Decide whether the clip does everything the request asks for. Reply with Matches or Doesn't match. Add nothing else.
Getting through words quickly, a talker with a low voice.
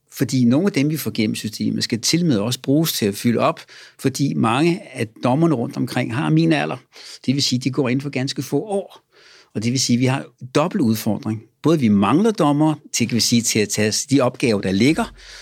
Matches